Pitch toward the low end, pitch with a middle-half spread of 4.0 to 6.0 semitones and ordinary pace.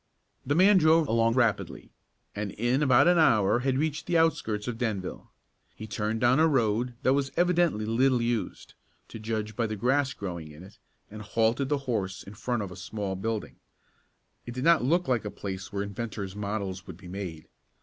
Yes: low, 115 Hz; average, 4.7 semitones; average, 190 wpm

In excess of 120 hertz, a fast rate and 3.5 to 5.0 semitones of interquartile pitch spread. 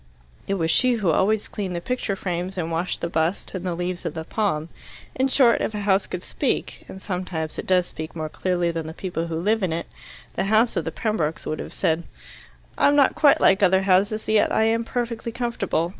Yes: medium, 185 Hz; fast, 225 wpm; average, 4.4 semitones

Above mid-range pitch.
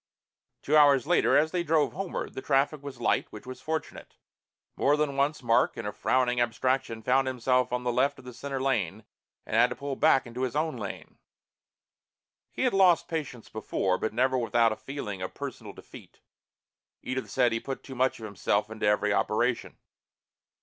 No: low, 130 Hz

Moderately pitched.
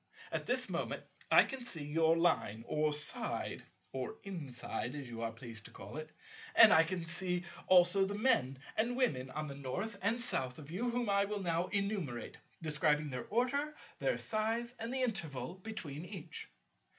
Yes: medium, 175 Hz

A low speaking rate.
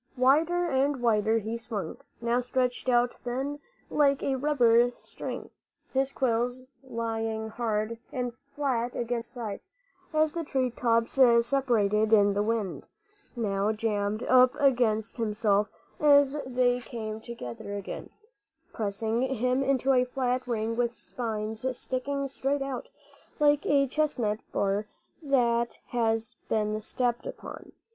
Yes: slow, 130 wpm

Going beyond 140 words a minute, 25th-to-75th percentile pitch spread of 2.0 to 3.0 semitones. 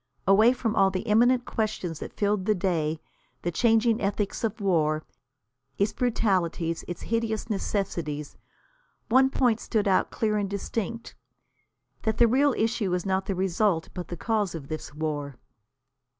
No: average, 150 wpm; average, 4.3 semitones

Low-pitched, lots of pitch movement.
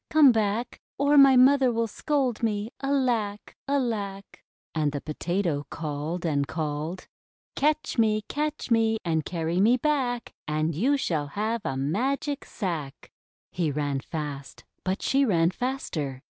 No: high, 205 Hz; wide, 8.5 semitones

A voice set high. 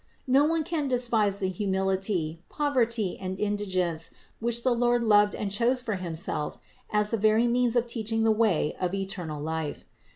Yes: high, 210 Hz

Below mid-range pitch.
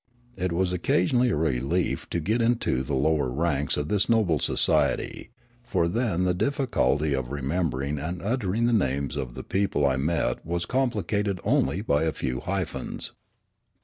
Yes: very low, 85 Hz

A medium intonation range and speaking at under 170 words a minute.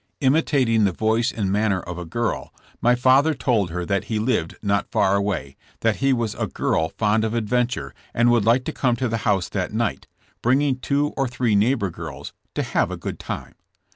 No: average, 4.1 semitones; fast, 205 wpm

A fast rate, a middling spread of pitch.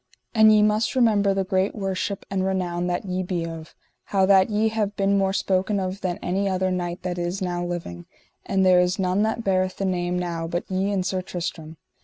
No: fast, 215 wpm; narrow, 1.9 semitones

